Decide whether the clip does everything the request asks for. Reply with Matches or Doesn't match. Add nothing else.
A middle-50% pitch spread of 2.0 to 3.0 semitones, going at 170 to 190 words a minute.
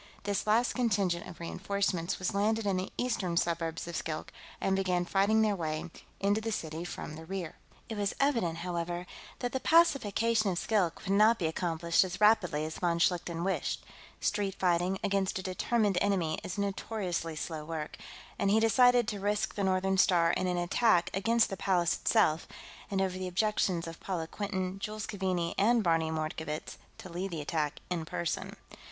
Doesn't match